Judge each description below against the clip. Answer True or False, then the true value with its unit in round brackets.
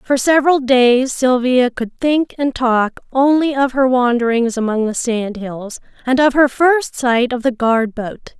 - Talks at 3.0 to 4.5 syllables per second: True (4.0 syllables/s)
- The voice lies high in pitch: True (250 Hz)